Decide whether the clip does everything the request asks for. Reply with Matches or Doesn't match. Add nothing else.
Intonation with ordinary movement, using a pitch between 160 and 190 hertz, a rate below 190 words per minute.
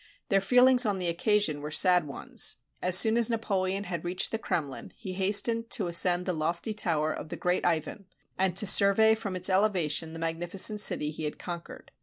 Doesn't match